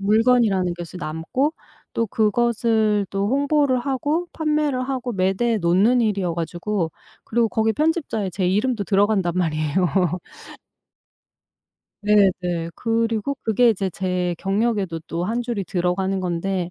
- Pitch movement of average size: Yes, average, 4.7 semitones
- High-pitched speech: Yes, high, 205 Hz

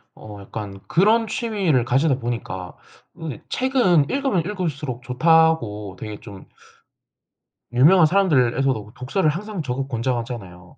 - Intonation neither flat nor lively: No, wide, 7.3 semitones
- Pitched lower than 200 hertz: Yes, low, 135 Hz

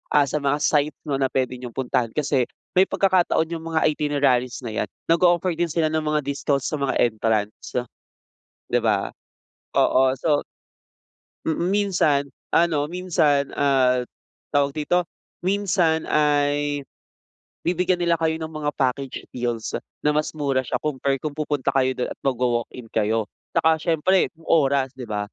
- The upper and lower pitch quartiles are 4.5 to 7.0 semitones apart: No, average, 3.7 semitones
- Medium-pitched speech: Yes, medium, 145 Hz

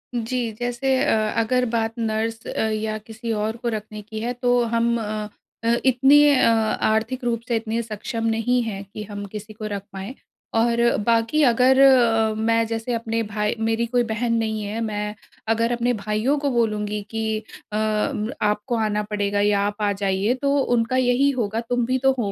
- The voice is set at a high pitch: Yes, high, 225 Hz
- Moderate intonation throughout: No, narrow, 2.0 semitones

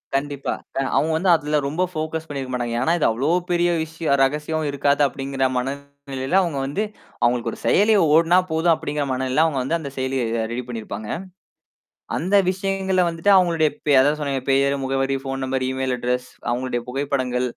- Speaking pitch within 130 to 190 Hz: Yes, medium, 140 Hz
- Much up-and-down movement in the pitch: No, average, 3.5 semitones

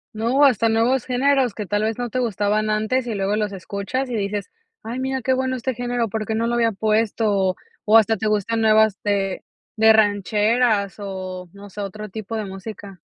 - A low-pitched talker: No, high, 220 Hz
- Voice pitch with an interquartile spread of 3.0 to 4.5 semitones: No, narrow, 2.6 semitones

